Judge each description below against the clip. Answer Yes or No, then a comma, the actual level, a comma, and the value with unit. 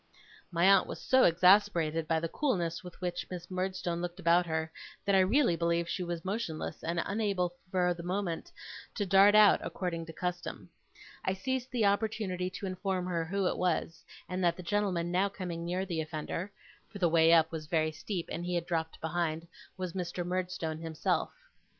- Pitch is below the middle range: No, medium, 180 Hz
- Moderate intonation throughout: No, narrow, 2.3 semitones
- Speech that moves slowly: No, average, 185 wpm